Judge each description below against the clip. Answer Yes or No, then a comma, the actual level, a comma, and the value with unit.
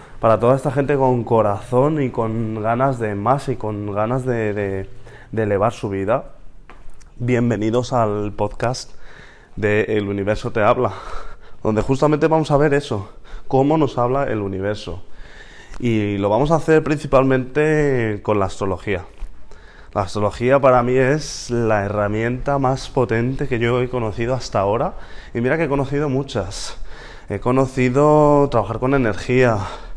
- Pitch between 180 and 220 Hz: No, low, 120 Hz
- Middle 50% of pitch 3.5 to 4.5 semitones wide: Yes, average, 4.1 semitones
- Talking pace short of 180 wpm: Yes, average, 150 wpm